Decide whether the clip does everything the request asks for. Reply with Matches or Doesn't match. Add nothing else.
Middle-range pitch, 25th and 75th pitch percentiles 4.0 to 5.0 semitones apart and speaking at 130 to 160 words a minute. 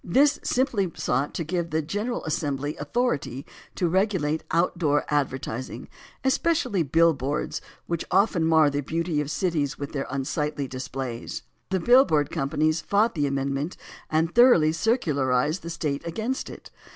Matches